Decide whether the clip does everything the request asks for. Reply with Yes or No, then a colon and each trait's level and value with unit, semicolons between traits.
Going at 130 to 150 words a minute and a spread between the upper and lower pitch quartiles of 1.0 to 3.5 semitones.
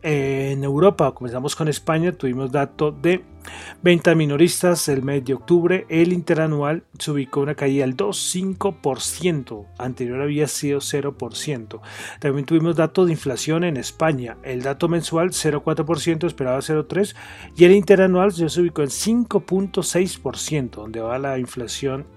No: average, 135 wpm; average, 4.1 semitones